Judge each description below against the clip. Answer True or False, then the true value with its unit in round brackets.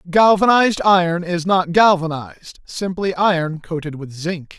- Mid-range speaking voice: True (175 Hz)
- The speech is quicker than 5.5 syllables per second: False (4.7 syllables/s)